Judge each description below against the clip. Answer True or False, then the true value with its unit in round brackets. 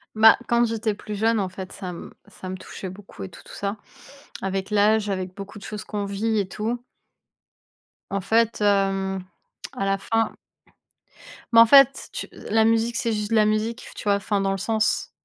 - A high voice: True (210 Hz)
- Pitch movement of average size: False (2.3 semitones)